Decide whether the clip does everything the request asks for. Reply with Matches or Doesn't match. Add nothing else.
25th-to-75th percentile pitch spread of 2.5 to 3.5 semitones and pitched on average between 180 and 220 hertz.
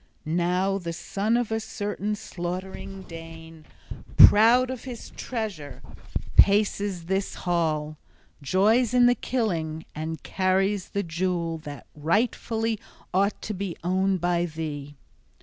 Doesn't match